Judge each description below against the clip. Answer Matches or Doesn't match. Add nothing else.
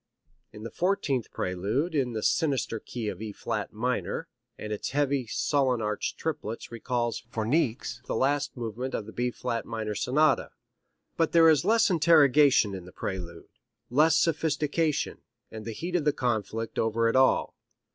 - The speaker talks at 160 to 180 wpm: Matches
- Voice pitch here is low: Matches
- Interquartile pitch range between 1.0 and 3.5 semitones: Doesn't match